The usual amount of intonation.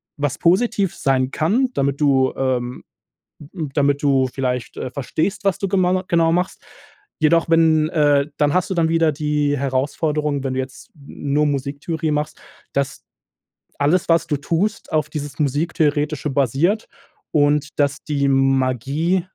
Yes: average, 3.0 semitones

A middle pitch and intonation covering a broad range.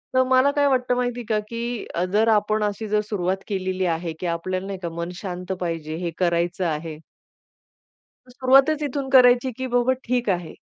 No: high, 210 Hz; wide, 5.9 semitones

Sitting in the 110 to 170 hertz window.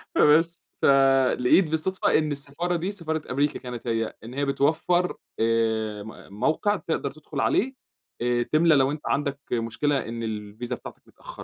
Yes: medium, 140 Hz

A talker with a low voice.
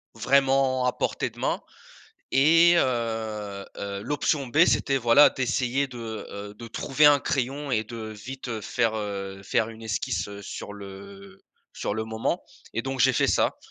Yes: low, 115 Hz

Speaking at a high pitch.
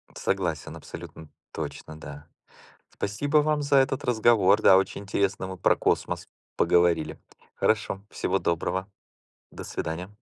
No: very low, 95 Hz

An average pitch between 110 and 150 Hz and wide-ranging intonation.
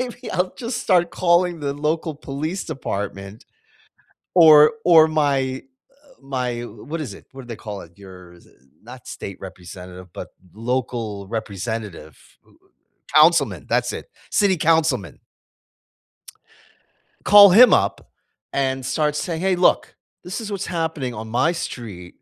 Yes: medium, 140 Hz; wide, 7.6 semitones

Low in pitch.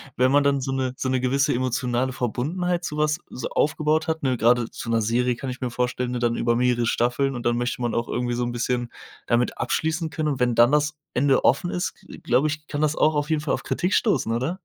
Yes: low, 130 Hz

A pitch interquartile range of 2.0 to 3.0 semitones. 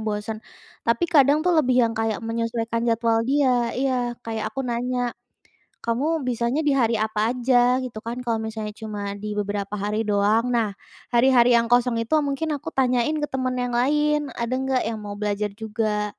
Yes: average, 2.7 semitones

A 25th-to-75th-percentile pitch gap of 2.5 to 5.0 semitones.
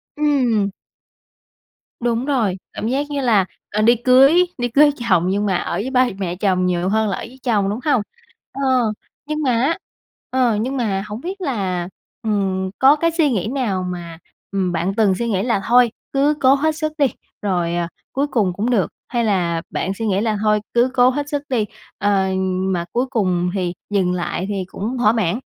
No: wide, 5.4 semitones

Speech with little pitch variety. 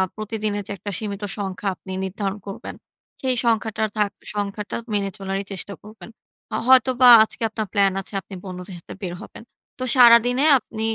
Yes: narrow, 2.3 semitones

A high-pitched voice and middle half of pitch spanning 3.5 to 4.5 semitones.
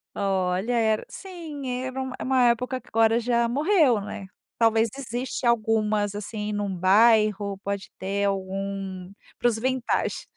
Yes: high, 220 Hz; average, 3.8 semitones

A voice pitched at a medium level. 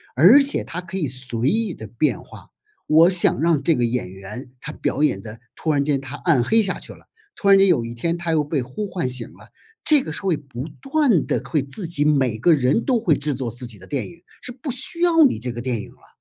Yes: medium, 150 Hz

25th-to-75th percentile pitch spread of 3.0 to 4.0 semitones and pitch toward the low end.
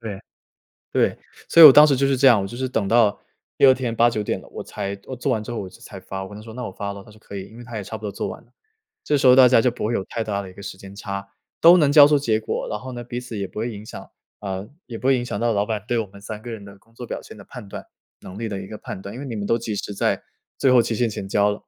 Yes: average, 3.5 semitones; low, 110 Hz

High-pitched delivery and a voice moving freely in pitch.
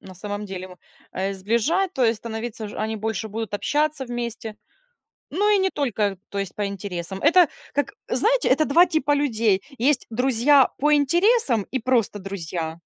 Yes: high, 230 Hz; wide, 6.3 semitones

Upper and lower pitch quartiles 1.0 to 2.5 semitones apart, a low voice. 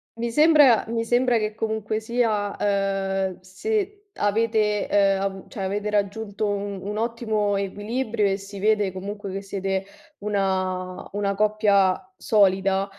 No: narrow, 2.1 semitones; high, 205 Hz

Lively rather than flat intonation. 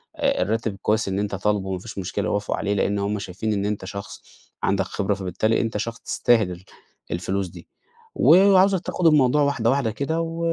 Yes: wide, 6.0 semitones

